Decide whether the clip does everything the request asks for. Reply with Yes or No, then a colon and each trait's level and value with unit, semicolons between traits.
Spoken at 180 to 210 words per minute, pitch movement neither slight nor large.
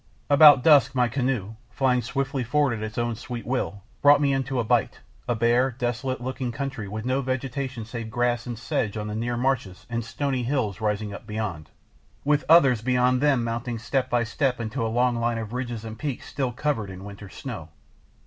Yes: average, 195 wpm; average, 3.0 semitones